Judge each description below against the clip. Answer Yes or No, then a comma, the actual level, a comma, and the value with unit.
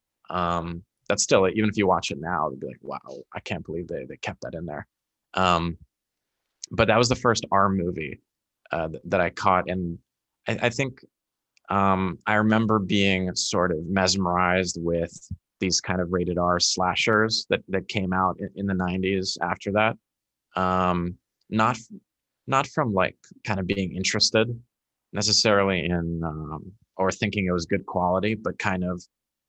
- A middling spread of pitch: Yes, average, 3.1 semitones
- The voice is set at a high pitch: No, very low, 95 Hz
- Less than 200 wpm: Yes, average, 170 wpm